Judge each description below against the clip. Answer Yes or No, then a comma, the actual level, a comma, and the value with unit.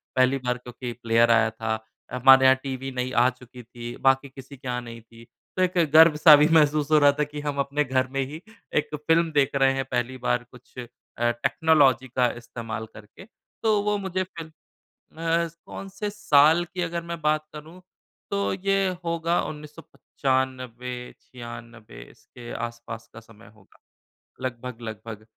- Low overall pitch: Yes, low, 130 Hz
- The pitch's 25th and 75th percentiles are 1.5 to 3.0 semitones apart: No, average, 4.3 semitones